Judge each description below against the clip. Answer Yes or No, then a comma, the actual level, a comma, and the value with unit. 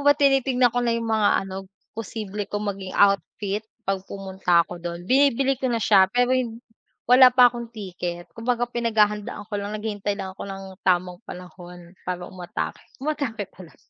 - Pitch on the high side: Yes, high, 210 Hz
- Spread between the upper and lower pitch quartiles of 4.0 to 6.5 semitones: Yes, average, 4.3 semitones